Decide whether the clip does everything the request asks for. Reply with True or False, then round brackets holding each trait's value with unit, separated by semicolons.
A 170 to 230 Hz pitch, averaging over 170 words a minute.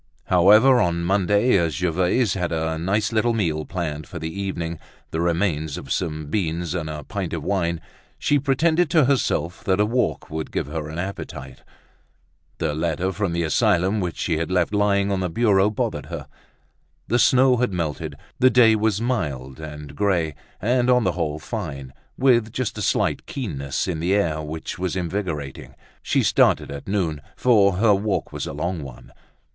False (90 Hz; 180 wpm)